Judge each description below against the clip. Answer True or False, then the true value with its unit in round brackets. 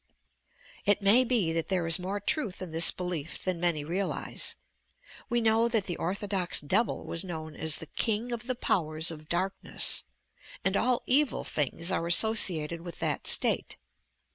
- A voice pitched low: False (185 Hz)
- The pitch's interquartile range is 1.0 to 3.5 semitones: False (4.9 semitones)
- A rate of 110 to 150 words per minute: False (165 wpm)